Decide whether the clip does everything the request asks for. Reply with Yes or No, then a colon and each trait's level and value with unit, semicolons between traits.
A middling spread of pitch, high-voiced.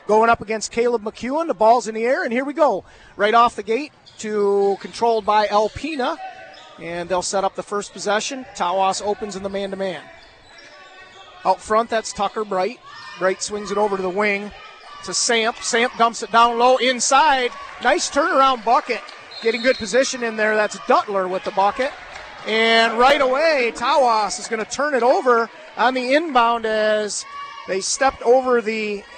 Yes: average, 3.8 semitones; high, 225 Hz